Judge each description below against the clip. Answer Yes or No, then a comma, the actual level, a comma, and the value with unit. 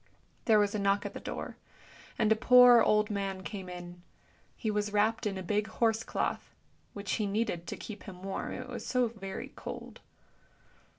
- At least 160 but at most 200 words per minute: Yes, average, 185 wpm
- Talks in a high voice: Yes, high, 210 Hz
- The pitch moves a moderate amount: No, narrow, 2.3 semitones